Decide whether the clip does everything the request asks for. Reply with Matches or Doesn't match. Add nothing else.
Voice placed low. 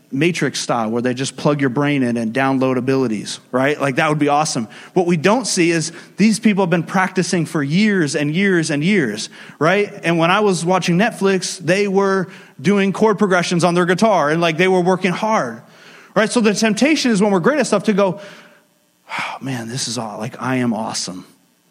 Doesn't match